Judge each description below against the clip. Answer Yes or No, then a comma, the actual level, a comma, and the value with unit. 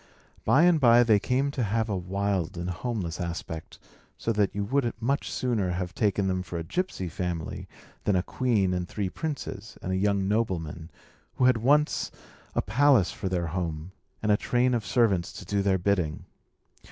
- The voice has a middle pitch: No, low, 100 Hz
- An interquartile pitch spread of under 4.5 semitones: No, average, 4.8 semitones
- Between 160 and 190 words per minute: Yes, average, 185 wpm